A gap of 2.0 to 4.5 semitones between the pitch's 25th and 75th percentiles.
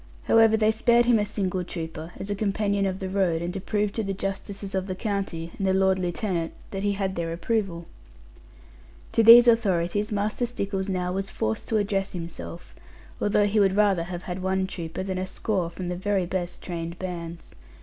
Yes: narrow, 2.6 semitones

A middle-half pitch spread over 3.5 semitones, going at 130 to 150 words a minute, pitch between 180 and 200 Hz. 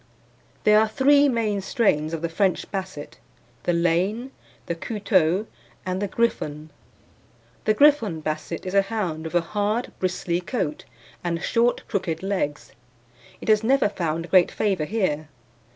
Yes: average, 4.6 semitones; average, 145 wpm; high, 190 Hz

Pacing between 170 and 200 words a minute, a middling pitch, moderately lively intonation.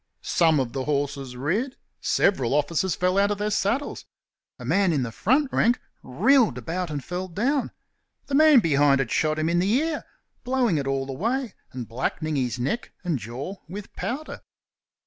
No: average, 175 wpm; medium, 170 Hz; wide, 8.4 semitones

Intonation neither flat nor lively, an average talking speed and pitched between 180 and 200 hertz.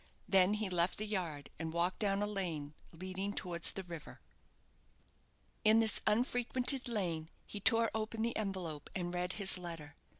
Yes: average, 3.9 semitones; average, 160 wpm; high, 190 Hz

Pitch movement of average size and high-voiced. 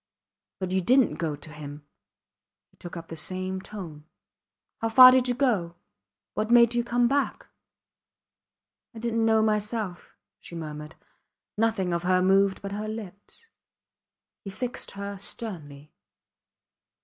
Yes: average, 4.8 semitones; high, 200 Hz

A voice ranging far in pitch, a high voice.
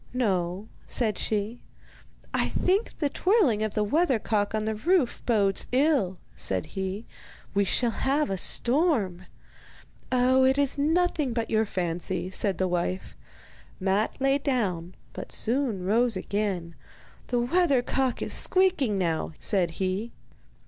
Yes: wide, 5.9 semitones; high, 220 Hz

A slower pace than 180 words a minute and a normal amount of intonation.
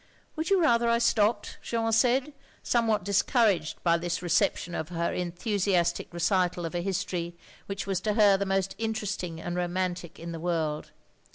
Yes: average, 165 wpm; average, 4.1 semitones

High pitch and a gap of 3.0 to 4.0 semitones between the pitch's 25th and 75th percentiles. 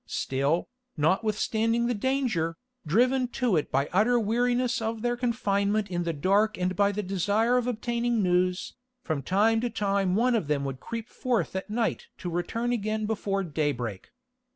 No: high, 210 Hz; average, 4.8 semitones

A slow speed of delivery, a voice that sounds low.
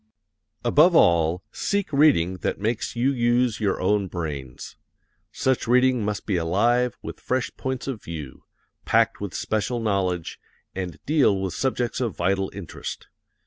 No: average, 145 wpm; low, 105 Hz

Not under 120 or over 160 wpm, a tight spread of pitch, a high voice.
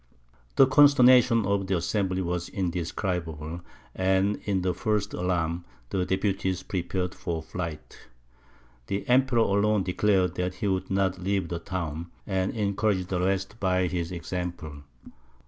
No: slow, 135 wpm; narrow, 2.2 semitones; very low, 95 Hz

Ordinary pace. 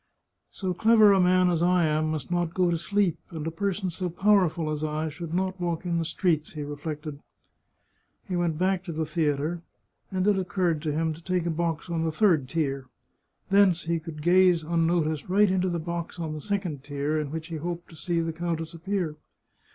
No: fast, 210 wpm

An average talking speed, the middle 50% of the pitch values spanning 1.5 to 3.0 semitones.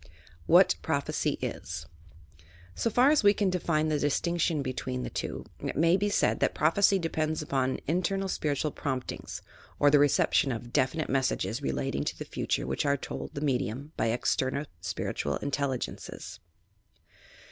No: average, 160 wpm; average, 4.5 semitones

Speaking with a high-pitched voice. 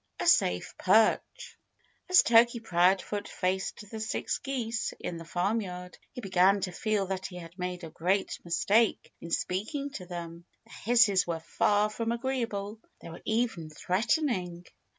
Yes: high, 195 Hz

